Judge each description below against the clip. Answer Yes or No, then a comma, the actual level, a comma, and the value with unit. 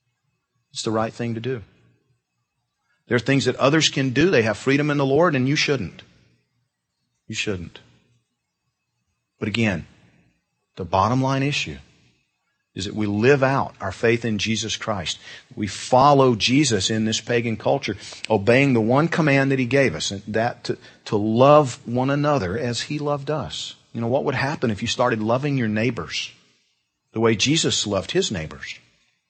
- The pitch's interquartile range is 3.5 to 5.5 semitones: Yes, average, 4.6 semitones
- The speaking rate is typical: Yes, average, 170 wpm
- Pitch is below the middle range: Yes, low, 120 Hz